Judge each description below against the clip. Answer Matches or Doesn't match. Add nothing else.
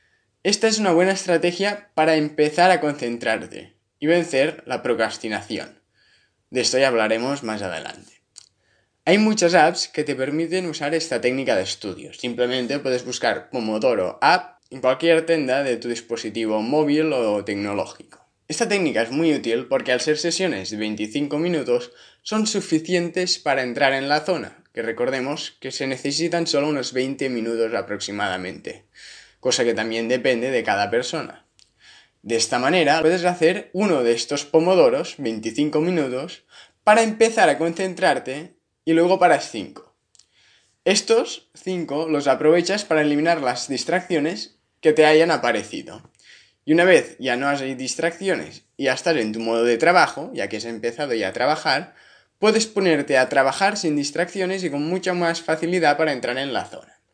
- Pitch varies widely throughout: Matches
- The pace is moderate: Matches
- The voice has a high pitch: Doesn't match